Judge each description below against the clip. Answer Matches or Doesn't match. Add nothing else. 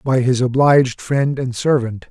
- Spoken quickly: Doesn't match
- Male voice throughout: Matches